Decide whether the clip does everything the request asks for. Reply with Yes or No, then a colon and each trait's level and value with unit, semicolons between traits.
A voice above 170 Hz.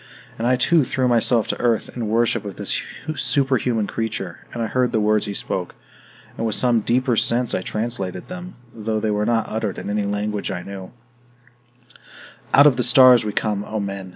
No: low, 110 Hz